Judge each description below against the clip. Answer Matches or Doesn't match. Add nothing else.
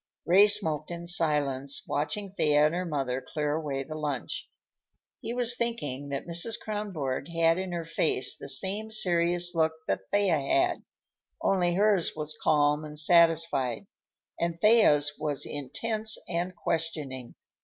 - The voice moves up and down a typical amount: Matches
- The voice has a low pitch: Doesn't match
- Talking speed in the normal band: Matches